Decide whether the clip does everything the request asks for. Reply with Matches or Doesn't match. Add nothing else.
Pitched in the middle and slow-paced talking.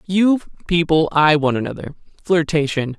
Matches